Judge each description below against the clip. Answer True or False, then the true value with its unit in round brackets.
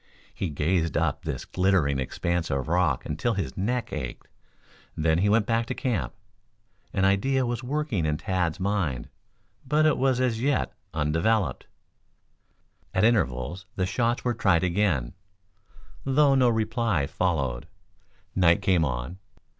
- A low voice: True (95 Hz)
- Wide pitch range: True (6.7 semitones)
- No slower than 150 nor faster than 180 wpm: False (140 wpm)